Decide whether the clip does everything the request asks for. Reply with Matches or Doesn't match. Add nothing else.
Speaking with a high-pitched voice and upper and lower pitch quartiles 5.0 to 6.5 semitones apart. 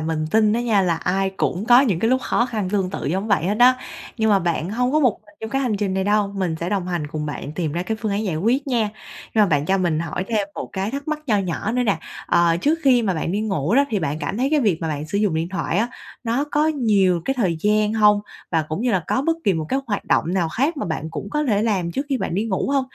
Matches